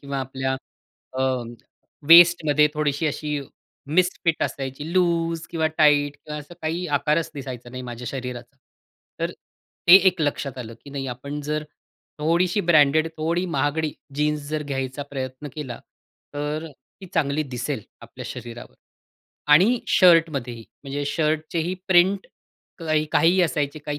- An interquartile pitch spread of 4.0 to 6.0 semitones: No, average, 3.3 semitones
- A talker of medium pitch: Yes, medium, 150 Hz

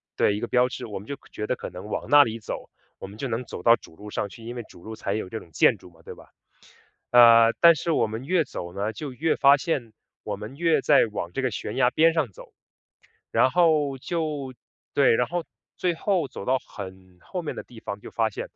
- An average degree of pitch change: No, wide, 5.7 semitones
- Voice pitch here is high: No, low, 120 Hz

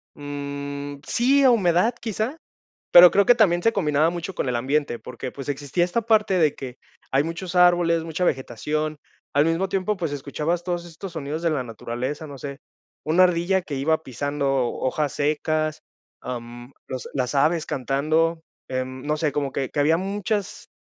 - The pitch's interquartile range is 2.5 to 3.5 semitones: No, average, 4.0 semitones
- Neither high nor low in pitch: Yes, medium, 155 Hz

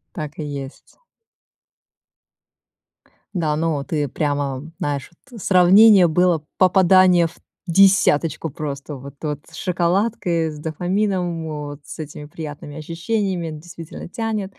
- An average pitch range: Yes, average, 3.7 semitones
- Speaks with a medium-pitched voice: Yes, medium, 165 Hz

